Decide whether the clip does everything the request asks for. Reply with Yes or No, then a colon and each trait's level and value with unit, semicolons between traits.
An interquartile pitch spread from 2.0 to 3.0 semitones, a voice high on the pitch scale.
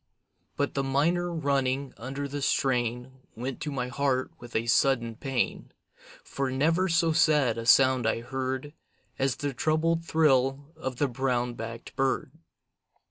No: narrow, 2.5 semitones; low, 135 Hz